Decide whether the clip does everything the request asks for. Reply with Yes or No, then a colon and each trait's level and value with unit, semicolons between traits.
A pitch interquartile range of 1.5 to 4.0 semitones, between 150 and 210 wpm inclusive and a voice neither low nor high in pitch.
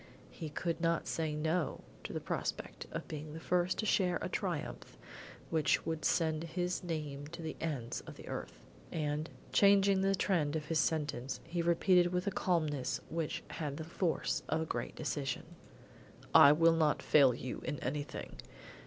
Yes: average, 2.7 semitones; average, 170 wpm; medium, 160 Hz